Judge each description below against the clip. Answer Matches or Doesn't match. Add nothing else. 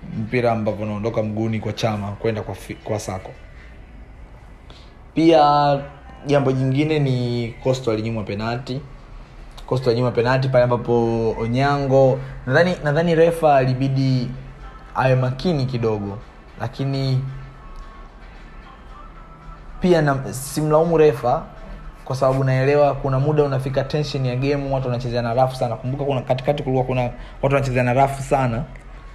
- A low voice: Matches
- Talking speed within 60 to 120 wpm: Matches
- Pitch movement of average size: Matches